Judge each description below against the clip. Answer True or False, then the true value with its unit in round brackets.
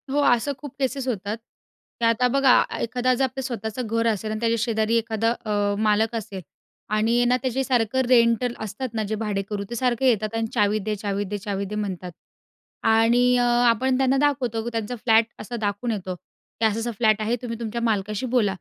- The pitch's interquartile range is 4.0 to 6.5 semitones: False (2.7 semitones)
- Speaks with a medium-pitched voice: False (225 Hz)